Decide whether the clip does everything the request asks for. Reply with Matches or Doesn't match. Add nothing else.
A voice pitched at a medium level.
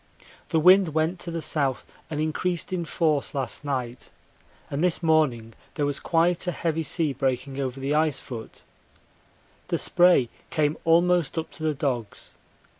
Matches